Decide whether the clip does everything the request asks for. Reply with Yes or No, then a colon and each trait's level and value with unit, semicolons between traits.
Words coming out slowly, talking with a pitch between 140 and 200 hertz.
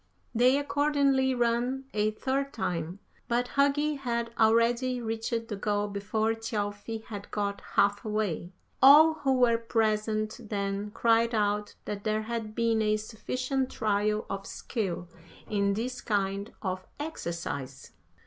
No: slow, 130 wpm; high, 220 Hz